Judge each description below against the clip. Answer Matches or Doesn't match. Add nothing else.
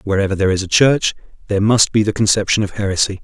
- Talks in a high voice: Doesn't match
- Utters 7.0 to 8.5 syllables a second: Matches